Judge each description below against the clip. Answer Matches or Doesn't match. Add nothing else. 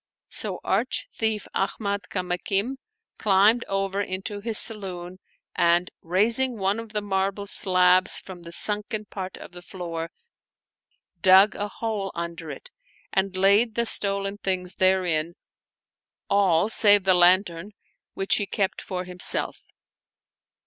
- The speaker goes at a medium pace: Doesn't match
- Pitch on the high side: Matches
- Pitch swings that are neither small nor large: Doesn't match